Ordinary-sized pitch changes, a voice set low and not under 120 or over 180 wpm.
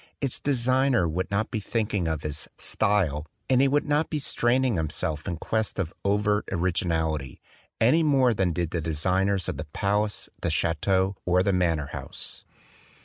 No: wide, 5.8 semitones; very low, 95 Hz; average, 170 wpm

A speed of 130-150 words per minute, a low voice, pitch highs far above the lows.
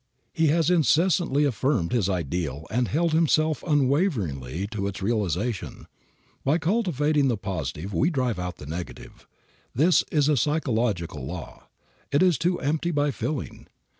Yes: average, 140 wpm; low, 130 Hz; wide, 8.8 semitones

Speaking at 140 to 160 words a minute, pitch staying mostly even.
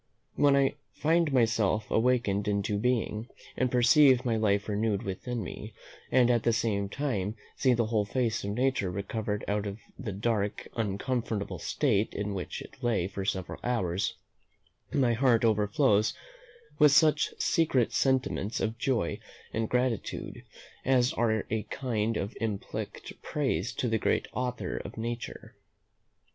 No: average, 145 wpm; average, 3.6 semitones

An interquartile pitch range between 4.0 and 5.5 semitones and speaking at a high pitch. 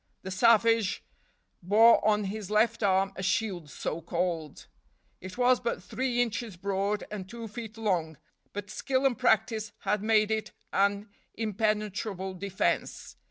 No: average, 3.0 semitones; high, 210 Hz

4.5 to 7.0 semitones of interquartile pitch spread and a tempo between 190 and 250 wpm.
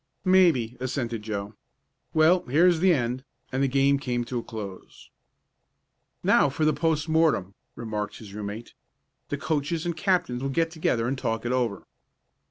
No: wide, 5.5 semitones; average, 165 wpm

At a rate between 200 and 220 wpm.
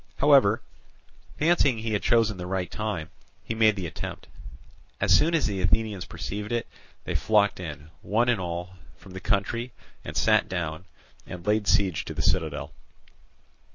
No: average, 160 wpm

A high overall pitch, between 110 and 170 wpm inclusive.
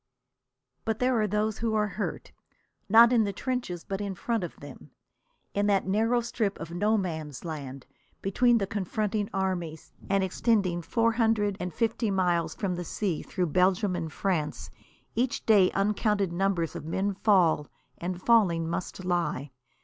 Yes: high, 195 Hz; average, 160 wpm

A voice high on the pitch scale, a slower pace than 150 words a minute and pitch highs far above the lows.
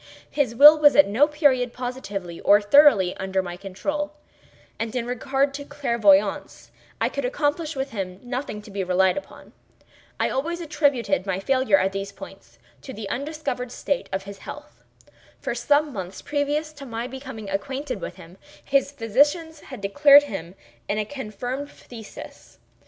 No: very high, 250 Hz; average, 160 wpm; wide, 6.4 semitones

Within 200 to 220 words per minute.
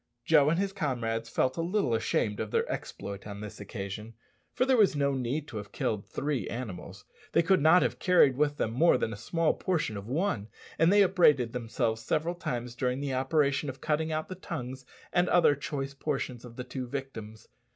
Yes: fast, 205 wpm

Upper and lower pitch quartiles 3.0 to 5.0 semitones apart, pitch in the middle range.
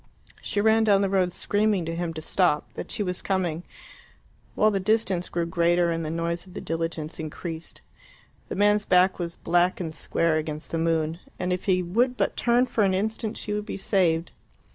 Yes: average, 3.5 semitones; medium, 180 Hz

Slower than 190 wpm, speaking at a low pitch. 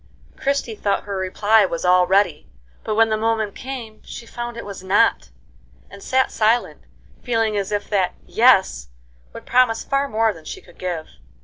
No: average, 175 wpm; high, 215 Hz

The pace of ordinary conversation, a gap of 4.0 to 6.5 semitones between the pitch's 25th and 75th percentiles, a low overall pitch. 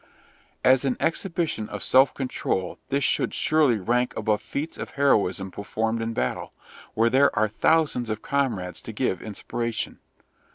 Yes: average, 150 wpm; average, 4.5 semitones; low, 115 Hz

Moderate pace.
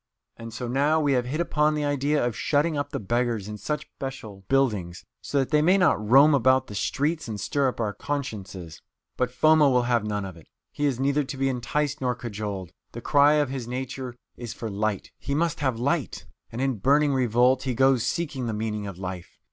No: fast, 215 wpm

